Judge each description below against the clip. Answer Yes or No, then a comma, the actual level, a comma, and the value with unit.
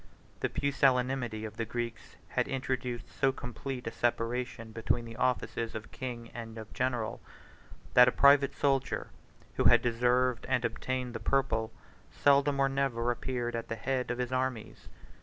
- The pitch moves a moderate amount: No, narrow, 2.1 semitones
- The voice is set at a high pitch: No, low, 125 Hz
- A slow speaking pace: No, average, 160 wpm